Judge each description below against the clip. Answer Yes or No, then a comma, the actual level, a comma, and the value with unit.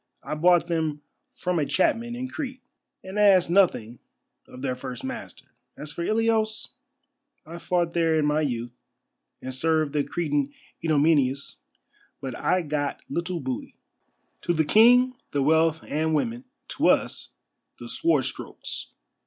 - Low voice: No, medium, 160 Hz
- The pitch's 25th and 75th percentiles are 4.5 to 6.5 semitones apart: Yes, average, 5.1 semitones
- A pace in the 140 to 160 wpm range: Yes, average, 145 wpm